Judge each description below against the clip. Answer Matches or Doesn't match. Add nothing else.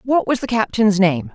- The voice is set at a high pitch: Matches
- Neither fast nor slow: Doesn't match